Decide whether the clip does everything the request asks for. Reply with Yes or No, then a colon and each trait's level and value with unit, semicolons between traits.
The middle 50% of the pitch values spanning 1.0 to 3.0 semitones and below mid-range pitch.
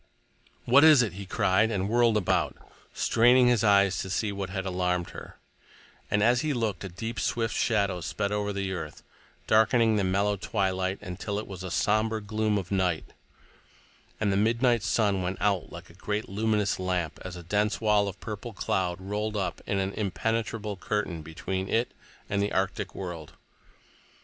Yes: narrow, 2.6 semitones; low, 100 Hz